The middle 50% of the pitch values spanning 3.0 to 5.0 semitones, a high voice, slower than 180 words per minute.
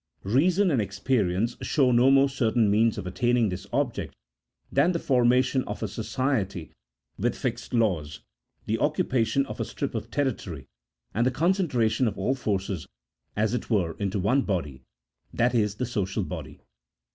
No: average, 4.7 semitones; low, 115 Hz; average, 160 wpm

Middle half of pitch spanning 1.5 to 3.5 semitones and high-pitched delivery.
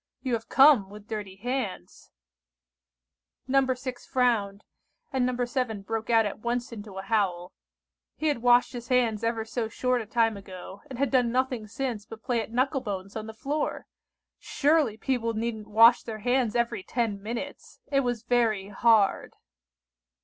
Yes: average, 2.9 semitones; high, 230 Hz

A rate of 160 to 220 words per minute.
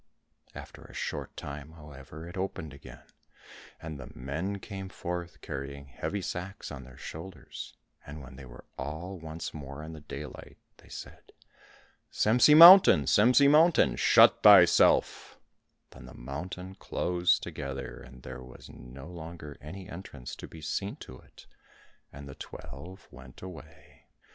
No: average, 145 wpm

